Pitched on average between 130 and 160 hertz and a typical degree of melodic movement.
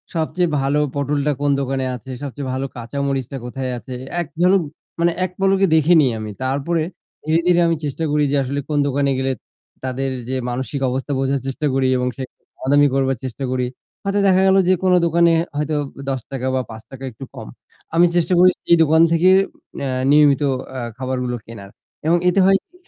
Yes: medium, 140 Hz; average, 4.0 semitones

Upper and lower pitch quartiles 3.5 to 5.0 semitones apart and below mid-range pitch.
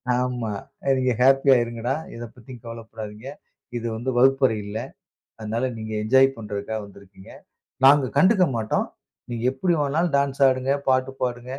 No: average, 3.1 semitones; low, 125 Hz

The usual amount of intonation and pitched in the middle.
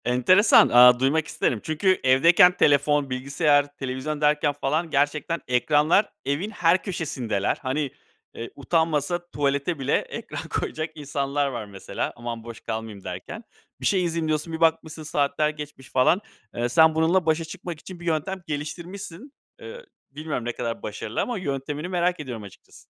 Yes: average, 3.9 semitones; medium, 150 Hz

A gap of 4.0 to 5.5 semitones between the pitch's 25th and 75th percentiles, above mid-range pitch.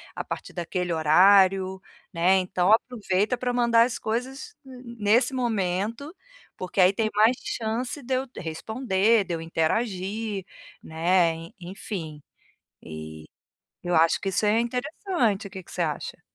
Yes: average, 4.9 semitones; high, 200 Hz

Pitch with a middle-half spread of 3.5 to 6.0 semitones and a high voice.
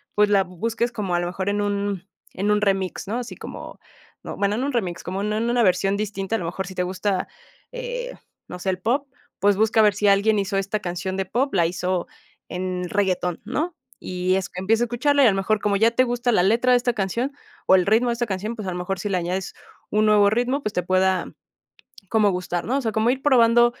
Yes: average, 3.9 semitones; high, 205 Hz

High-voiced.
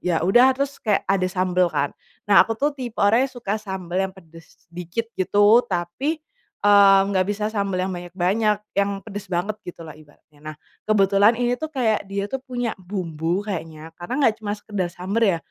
Yes: high, 200 Hz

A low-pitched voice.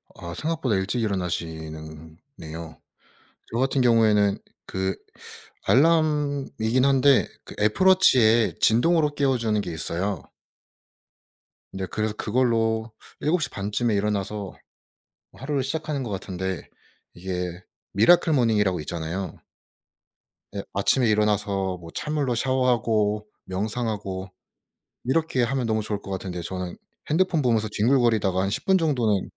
Yes: low, 110 Hz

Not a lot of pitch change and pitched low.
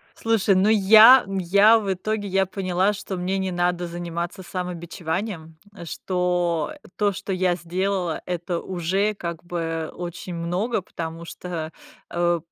No: narrow, 2.3 semitones; medium, 180 Hz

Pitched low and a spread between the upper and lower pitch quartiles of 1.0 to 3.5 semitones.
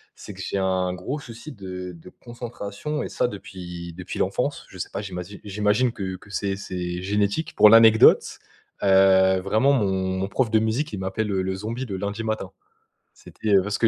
Yes: low, 100 Hz; average, 2.9 semitones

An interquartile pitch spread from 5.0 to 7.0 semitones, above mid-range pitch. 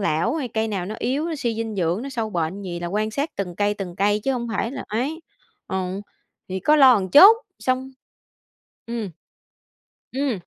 Yes: wide, 5.5 semitones; high, 220 Hz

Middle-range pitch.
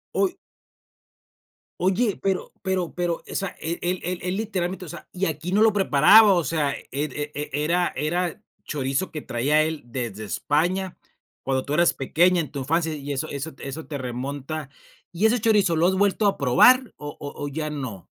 Yes: medium, 160 Hz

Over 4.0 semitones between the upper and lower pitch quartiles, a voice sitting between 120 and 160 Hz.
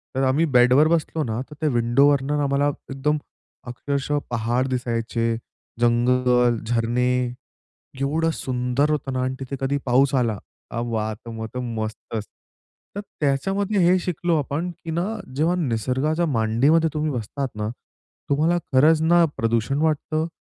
Yes: average, 4.4 semitones; low, 135 Hz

